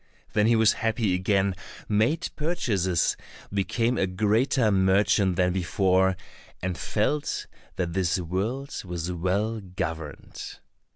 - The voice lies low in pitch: Yes, very low, 95 Hz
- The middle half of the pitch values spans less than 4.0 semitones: Yes, average, 3.4 semitones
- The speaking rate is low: Yes, slow, 115 wpm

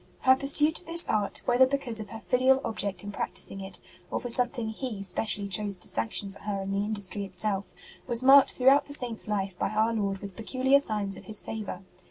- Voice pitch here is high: Yes, high, 215 Hz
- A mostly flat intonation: No, average, 4.4 semitones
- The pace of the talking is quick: Yes, fast, 225 wpm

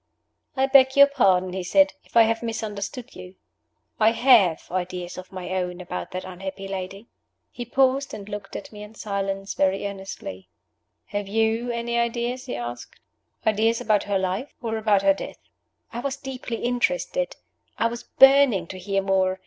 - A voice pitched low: No, high, 210 Hz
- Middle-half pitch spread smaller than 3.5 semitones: No, average, 4.1 semitones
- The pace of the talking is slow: No, average, 170 wpm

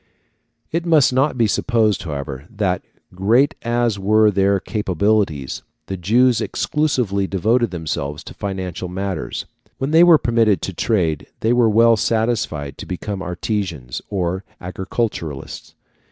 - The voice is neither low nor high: No, low, 100 Hz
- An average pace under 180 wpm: Yes, slow, 135 wpm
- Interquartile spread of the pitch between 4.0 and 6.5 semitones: Yes, average, 4.5 semitones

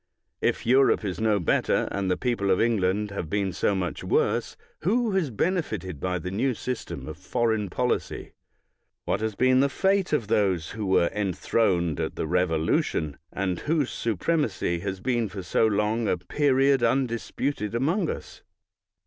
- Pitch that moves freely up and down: Yes, wide, 5.7 semitones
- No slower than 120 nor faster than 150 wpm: No, average, 160 wpm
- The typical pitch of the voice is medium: No, low, 105 Hz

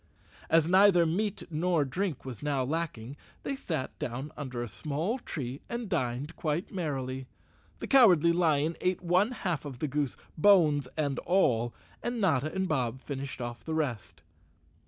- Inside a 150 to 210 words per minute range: Yes, average, 155 wpm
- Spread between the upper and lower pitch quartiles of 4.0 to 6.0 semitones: Yes, wide, 5.4 semitones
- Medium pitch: Yes, medium, 155 Hz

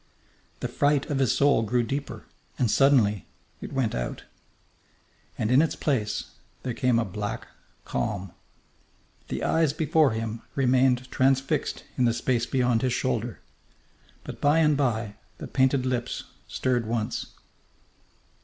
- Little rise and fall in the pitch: No, average, 3.3 semitones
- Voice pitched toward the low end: Yes, low, 125 Hz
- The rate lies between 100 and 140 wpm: Yes, slow, 135 wpm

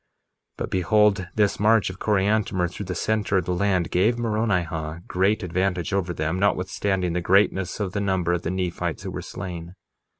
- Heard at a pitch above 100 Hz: No, very low, 95 Hz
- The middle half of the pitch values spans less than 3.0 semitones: Yes, narrow, 2.5 semitones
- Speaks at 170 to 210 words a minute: Yes, average, 180 wpm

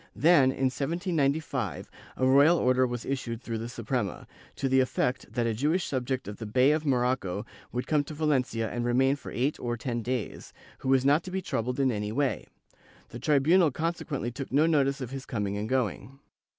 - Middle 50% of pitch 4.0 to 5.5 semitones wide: No, average, 3.0 semitones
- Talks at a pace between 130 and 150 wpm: No, average, 195 wpm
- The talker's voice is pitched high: No, low, 130 Hz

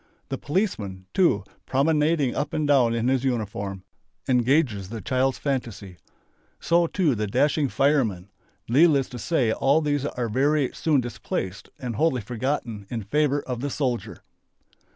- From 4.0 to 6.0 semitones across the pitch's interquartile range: Yes, average, 4.4 semitones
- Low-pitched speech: Yes, low, 130 Hz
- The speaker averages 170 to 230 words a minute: No, average, 145 wpm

